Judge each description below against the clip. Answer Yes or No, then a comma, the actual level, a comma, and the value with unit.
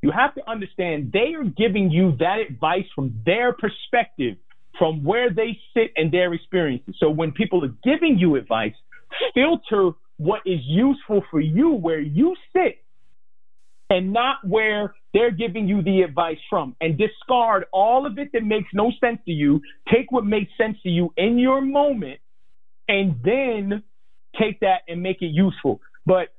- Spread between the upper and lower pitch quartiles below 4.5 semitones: No, wide, 5.4 semitones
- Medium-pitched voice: No, high, 205 Hz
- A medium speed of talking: Yes, average, 170 wpm